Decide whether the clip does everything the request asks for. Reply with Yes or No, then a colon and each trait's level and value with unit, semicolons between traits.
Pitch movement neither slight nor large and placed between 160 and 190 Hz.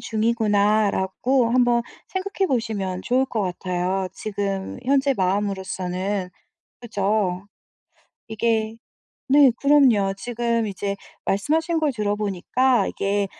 No: average, 4.0 semitones; high, 215 Hz